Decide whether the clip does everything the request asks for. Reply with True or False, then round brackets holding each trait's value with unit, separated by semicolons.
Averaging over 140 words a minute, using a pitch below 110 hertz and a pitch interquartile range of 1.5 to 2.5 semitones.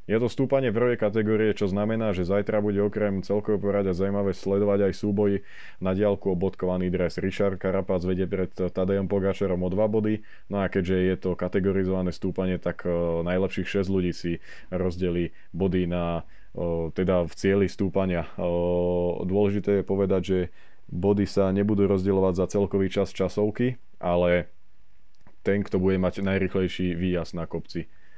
True (150 wpm; 95 Hz; 1.8 semitones)